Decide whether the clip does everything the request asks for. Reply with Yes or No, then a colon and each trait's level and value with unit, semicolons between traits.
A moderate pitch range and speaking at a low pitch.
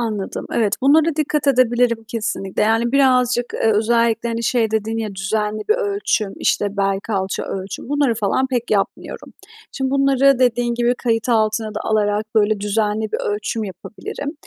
No: average, 3.0 semitones; high, 225 Hz